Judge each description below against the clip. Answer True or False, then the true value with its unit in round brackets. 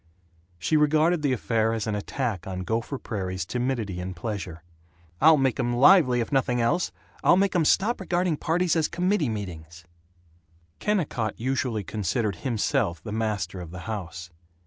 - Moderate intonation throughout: False (7.8 semitones)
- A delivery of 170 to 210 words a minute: False (155 wpm)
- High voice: False (115 Hz)